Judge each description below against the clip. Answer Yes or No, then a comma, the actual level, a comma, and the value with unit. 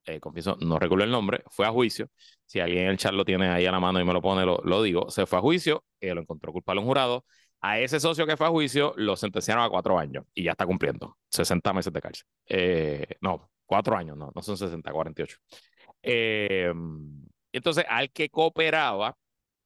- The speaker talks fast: Yes, fast, 220 wpm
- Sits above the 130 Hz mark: No, low, 100 Hz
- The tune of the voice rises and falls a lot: Yes, wide, 7.7 semitones